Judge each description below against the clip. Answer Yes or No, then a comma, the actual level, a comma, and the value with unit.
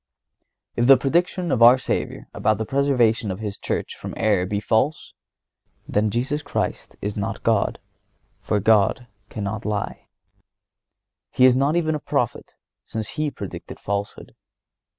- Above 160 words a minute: No, average, 145 wpm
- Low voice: Yes, low, 115 Hz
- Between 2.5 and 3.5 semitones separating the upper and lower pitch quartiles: No, average, 4.9 semitones